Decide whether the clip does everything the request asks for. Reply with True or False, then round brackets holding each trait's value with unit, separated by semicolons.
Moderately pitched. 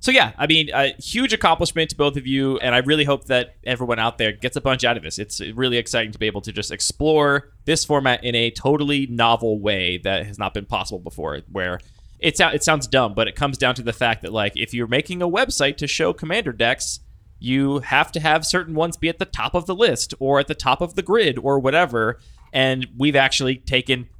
False (130 Hz)